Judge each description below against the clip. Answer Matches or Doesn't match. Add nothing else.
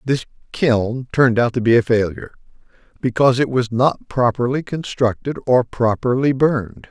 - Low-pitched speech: Matches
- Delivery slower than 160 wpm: Matches